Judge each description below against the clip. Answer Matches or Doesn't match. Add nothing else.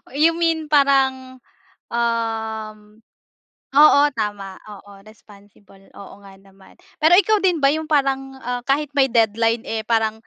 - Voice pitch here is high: Matches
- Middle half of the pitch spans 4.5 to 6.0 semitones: Matches